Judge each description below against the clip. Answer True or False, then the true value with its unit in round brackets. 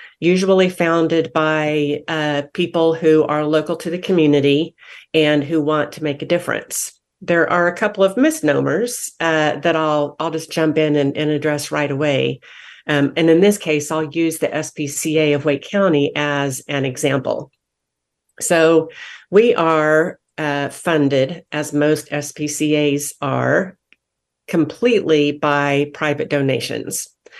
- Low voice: False (155 Hz)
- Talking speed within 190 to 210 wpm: False (140 wpm)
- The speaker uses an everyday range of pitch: False (2.1 semitones)